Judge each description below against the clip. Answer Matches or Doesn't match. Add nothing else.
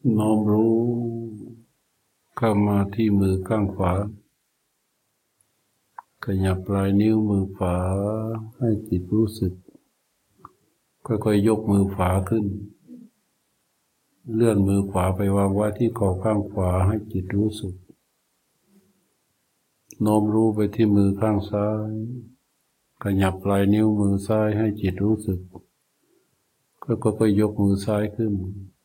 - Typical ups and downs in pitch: Doesn't match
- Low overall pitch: Matches